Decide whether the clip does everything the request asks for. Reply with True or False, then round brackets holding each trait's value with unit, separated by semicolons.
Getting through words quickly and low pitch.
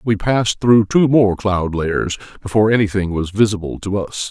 False (180 wpm; 100 Hz)